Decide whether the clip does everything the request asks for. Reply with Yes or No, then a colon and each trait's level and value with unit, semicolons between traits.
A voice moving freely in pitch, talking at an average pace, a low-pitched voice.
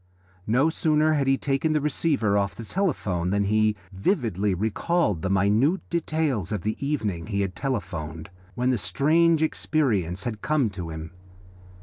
Yes: wide, 7.6 semitones; average, 155 wpm; low, 110 Hz